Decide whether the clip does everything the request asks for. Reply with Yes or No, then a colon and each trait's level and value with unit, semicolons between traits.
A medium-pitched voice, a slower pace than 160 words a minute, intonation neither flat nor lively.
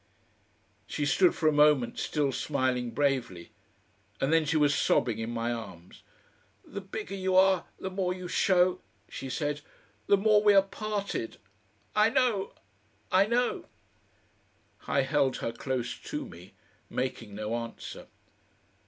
No: medium, 150 Hz; average, 145 wpm; wide, 7.8 semitones